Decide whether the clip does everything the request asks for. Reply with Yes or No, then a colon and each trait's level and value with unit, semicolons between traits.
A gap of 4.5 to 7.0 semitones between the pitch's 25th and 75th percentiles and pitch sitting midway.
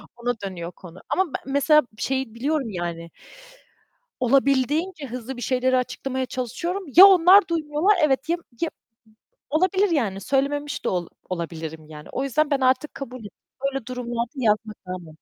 No: wide, 5.6 semitones; very high, 260 Hz